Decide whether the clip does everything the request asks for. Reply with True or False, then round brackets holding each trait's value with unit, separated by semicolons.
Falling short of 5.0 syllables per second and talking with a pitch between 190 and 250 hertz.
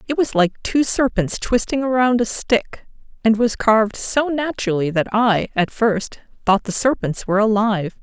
True (4.7 syllables/s; 225 Hz)